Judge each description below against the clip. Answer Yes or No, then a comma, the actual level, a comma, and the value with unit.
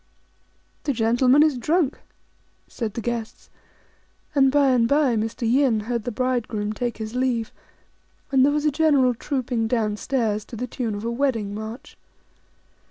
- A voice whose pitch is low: No, high, 245 Hz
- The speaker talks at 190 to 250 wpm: No, average, 160 wpm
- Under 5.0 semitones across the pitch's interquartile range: Yes, average, 3.3 semitones